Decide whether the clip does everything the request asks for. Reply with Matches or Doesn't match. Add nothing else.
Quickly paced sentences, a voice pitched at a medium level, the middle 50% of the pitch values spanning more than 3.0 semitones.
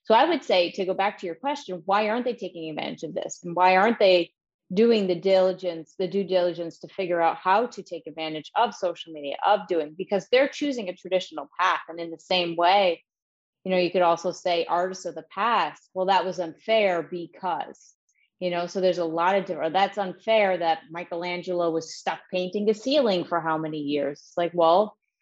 Doesn't match